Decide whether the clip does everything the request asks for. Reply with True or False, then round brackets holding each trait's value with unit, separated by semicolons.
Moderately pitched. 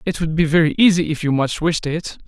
True (160 Hz)